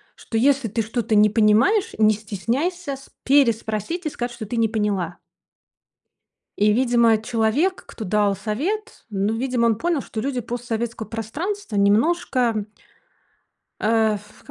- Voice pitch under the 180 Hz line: No, high, 230 Hz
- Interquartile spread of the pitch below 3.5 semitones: No, average, 3.9 semitones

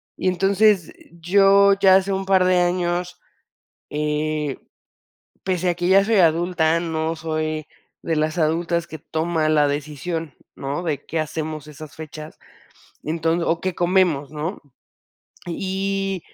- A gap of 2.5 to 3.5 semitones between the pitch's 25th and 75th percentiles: Yes, average, 2.9 semitones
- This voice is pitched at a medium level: Yes, medium, 170 Hz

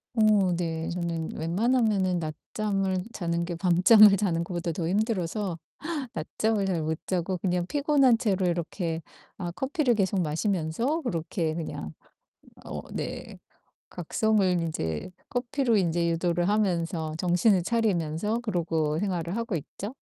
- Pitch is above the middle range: No, medium, 180 Hz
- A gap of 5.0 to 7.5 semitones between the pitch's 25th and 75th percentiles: No, average, 4.2 semitones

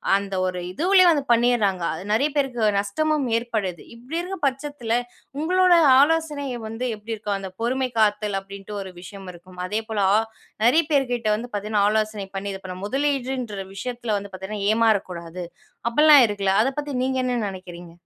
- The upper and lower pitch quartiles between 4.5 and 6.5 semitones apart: Yes, average, 5.2 semitones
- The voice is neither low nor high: No, high, 220 Hz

